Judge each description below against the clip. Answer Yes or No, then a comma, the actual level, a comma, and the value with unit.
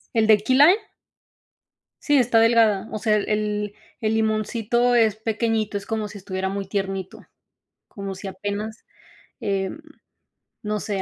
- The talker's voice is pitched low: No, high, 215 Hz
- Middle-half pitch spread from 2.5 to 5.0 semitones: No, narrow, 2.0 semitones